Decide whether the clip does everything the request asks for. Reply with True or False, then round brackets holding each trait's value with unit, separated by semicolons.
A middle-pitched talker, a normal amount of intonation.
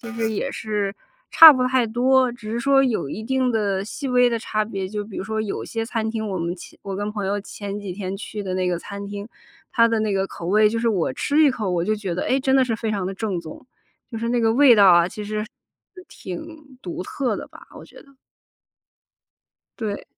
False (215 Hz; 3.3 semitones)